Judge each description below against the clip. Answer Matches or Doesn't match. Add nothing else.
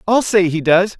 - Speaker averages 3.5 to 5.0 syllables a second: Matches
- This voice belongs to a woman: Doesn't match